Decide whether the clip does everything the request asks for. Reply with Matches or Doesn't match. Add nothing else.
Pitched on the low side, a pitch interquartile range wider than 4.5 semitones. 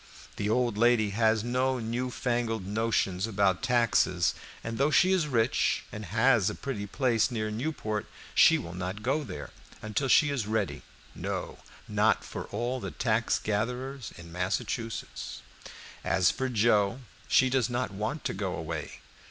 Doesn't match